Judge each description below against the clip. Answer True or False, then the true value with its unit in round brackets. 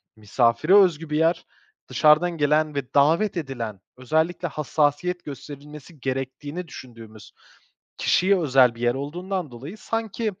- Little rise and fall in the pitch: False (4.9 semitones)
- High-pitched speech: False (150 Hz)